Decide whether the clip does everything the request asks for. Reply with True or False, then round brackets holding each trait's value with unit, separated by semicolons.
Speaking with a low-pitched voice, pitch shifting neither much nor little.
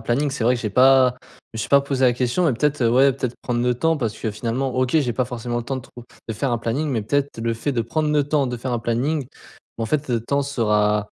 True (125 Hz; 3.2 semitones)